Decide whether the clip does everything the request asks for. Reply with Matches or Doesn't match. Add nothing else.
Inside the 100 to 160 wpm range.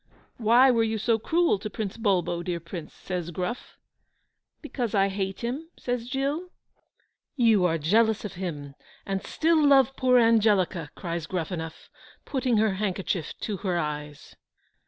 Matches